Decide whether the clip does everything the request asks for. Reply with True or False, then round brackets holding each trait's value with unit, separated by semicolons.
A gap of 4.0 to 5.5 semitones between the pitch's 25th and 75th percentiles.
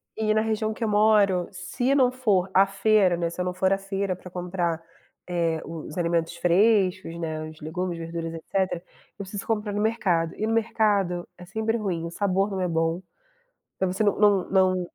False (3.5 semitones)